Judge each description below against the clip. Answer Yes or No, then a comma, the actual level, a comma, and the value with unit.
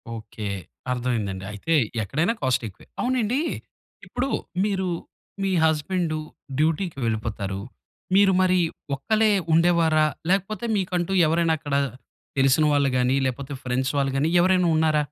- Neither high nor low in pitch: Yes, medium, 155 Hz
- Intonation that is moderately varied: No, wide, 6.3 semitones